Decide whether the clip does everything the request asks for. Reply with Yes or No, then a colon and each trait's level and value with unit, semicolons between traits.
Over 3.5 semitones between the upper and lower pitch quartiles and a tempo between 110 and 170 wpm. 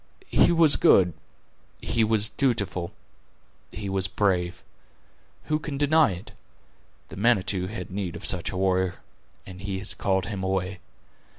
No: average, 3.2 semitones; average, 140 wpm